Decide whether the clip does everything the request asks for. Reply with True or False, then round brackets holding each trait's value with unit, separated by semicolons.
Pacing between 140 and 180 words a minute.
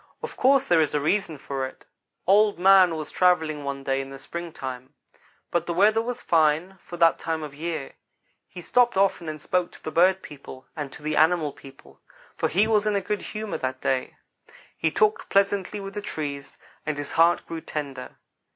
False (195 wpm)